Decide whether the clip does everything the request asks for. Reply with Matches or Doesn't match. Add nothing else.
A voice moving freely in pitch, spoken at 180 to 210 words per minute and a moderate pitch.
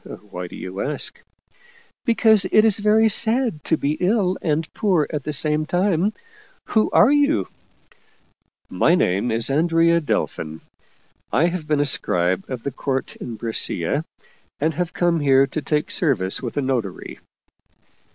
Doesn't match